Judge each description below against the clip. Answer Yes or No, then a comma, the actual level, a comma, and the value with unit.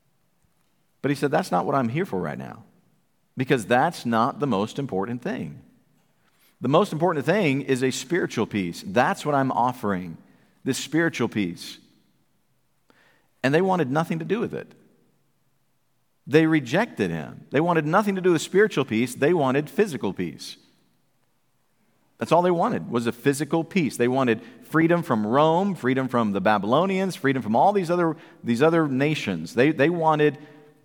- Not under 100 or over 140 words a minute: No, average, 165 wpm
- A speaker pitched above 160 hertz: No, medium, 150 Hz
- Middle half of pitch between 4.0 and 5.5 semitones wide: Yes, average, 5.1 semitones